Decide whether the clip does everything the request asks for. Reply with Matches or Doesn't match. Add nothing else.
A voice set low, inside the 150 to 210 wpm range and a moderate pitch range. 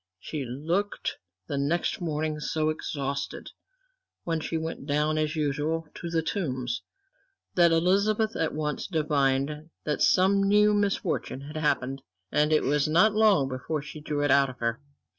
Doesn't match